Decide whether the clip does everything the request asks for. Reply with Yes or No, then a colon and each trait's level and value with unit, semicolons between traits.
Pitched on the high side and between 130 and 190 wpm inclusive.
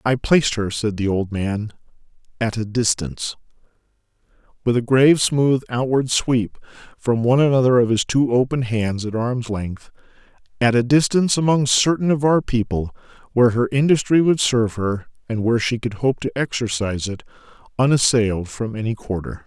No: low, 120 Hz; average, 160 wpm